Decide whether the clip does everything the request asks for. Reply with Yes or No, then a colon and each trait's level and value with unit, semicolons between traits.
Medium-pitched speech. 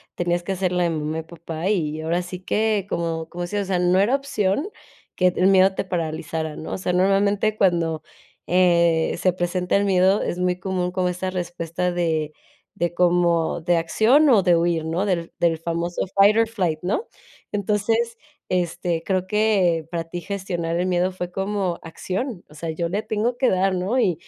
Yes: medium, 180 Hz